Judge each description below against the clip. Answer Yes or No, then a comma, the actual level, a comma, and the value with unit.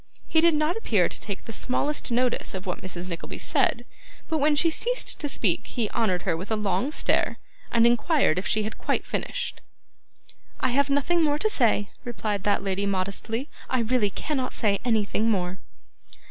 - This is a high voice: Yes, high, 230 Hz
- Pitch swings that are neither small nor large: No, wide, 6.5 semitones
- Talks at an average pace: Yes, average, 185 wpm